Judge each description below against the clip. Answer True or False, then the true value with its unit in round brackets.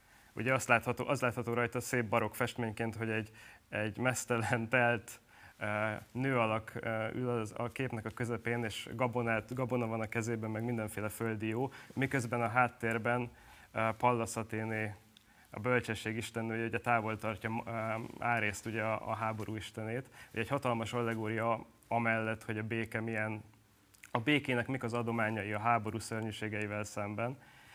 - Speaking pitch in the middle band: False (115 Hz)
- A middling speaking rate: True (145 wpm)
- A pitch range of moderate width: False (1.7 semitones)